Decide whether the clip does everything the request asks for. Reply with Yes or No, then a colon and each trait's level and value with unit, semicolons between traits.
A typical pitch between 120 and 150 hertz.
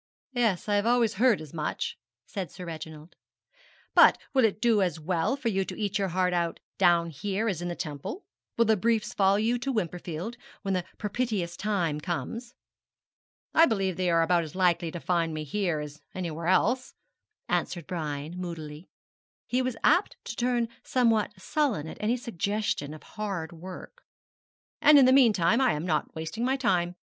No: high, 190 Hz